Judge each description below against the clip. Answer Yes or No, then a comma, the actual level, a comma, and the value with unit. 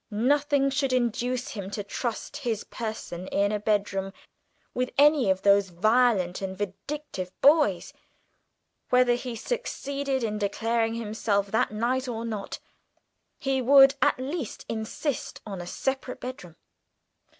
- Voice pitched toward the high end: Yes, high, 230 Hz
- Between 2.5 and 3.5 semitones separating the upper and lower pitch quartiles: No, average, 4.6 semitones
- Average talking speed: No, slow, 130 wpm